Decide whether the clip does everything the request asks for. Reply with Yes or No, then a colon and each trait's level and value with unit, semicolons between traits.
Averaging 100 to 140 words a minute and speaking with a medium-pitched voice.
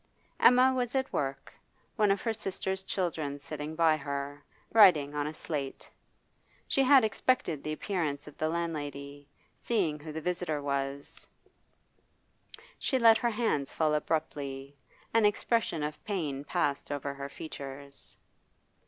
Yes: slow, 135 wpm; medium, 155 Hz